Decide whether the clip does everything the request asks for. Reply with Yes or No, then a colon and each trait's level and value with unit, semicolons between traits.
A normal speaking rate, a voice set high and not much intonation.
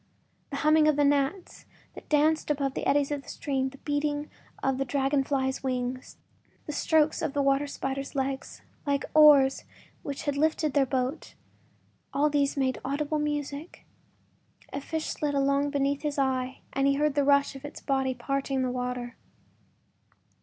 Yes: average, 165 wpm; very high, 280 Hz; narrow, 1.6 semitones